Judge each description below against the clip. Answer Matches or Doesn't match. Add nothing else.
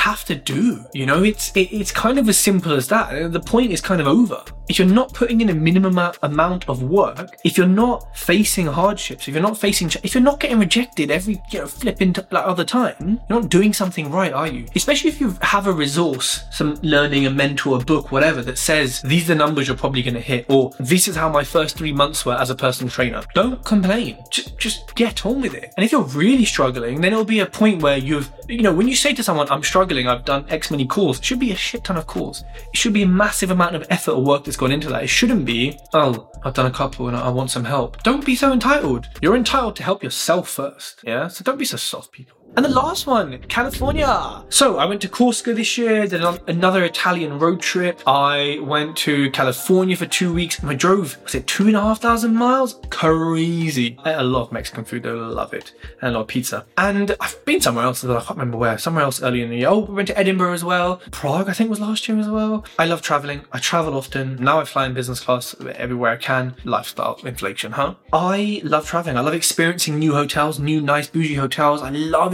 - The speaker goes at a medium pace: Doesn't match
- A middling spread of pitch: Doesn't match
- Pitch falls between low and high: Matches